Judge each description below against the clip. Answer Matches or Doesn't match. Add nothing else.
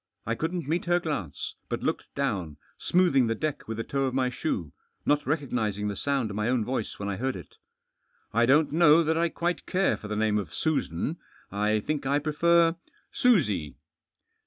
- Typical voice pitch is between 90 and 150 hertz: Matches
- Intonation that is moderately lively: Doesn't match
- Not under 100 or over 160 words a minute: Doesn't match